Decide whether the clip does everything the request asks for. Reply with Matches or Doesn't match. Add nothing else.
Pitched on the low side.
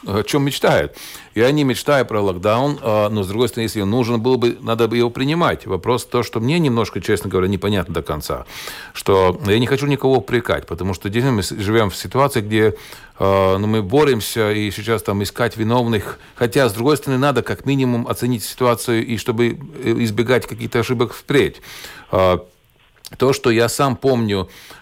Matches